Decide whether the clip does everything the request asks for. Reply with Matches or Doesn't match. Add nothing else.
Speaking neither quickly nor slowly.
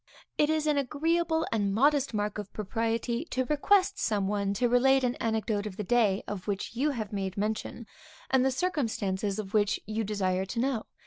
Matches